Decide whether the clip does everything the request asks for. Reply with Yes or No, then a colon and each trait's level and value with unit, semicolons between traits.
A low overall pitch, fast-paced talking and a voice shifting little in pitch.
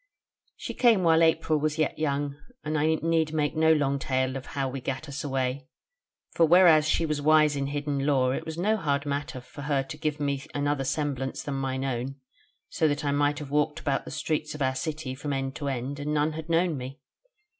No: medium, 145 Hz; fast, 220 wpm; narrow, 2.3 semitones